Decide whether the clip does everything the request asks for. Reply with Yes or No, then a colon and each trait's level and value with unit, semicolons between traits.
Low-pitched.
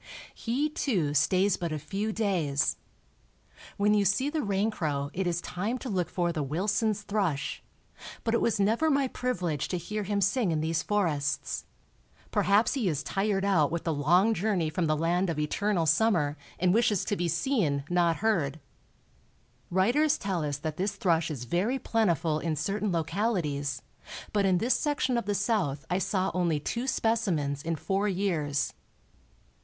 No: medium, 185 Hz